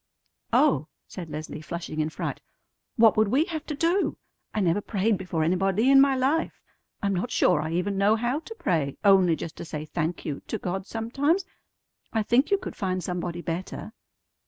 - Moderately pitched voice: No, high, 195 Hz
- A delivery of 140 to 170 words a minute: No, average, 185 wpm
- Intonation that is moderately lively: No, wide, 6.4 semitones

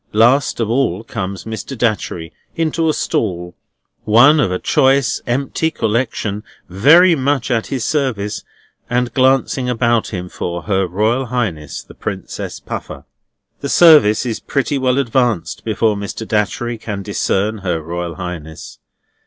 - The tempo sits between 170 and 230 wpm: No, average, 140 wpm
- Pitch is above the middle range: No, low, 115 Hz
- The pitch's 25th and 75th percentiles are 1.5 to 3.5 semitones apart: No, average, 5.0 semitones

